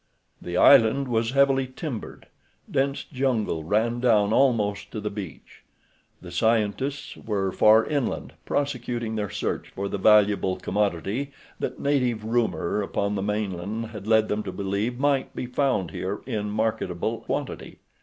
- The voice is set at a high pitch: No, low, 110 Hz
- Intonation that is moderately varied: Yes, average, 3.7 semitones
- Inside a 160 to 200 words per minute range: No, average, 145 wpm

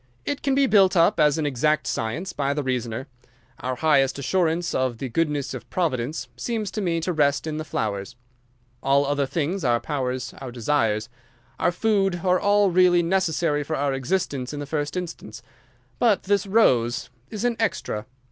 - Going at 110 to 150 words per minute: No, average, 175 wpm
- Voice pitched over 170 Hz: No, medium, 150 Hz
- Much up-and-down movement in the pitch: Yes, wide, 5.8 semitones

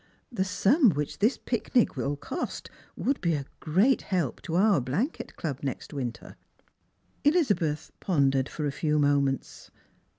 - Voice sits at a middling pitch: Yes, medium, 160 Hz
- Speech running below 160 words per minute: Yes, average, 140 wpm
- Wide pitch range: Yes, wide, 6.9 semitones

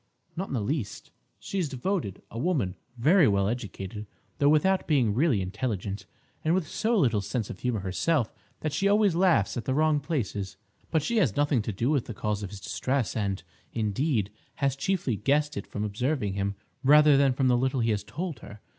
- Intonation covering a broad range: Yes, wide, 6.7 semitones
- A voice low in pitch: Yes, low, 130 Hz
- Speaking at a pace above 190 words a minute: Yes, average, 200 wpm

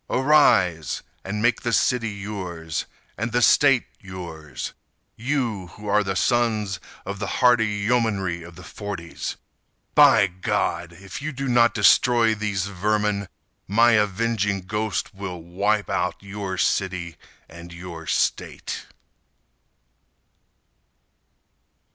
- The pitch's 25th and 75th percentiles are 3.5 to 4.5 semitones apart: Yes, average, 3.8 semitones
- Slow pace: Yes, slow, 110 wpm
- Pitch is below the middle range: Yes, low, 100 Hz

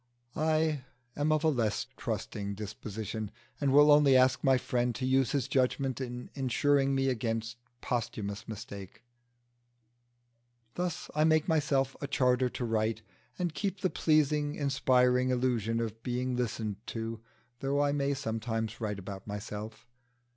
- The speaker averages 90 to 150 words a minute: Yes, average, 140 wpm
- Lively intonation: No, average, 4.2 semitones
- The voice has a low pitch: Yes, low, 125 Hz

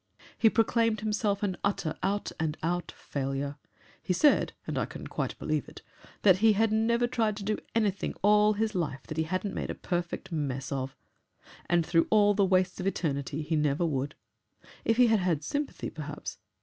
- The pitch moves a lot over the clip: Yes, wide, 5.8 semitones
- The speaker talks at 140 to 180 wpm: No, average, 190 wpm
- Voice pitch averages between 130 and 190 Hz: Yes, medium, 185 Hz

